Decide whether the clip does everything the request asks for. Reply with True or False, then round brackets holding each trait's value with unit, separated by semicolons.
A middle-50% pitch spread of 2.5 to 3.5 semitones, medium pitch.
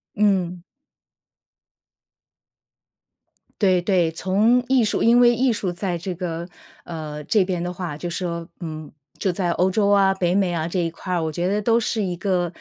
True (2.9 semitones; 180 Hz)